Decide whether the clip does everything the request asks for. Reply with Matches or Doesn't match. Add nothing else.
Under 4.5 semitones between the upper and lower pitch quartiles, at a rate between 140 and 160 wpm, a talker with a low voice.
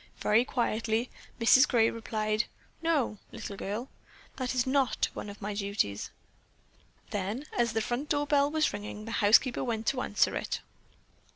Doesn't match